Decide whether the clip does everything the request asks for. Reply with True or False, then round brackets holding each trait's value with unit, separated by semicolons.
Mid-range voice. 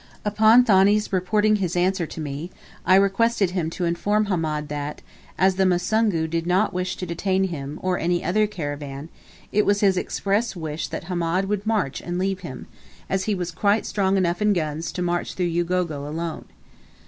True (180 Hz)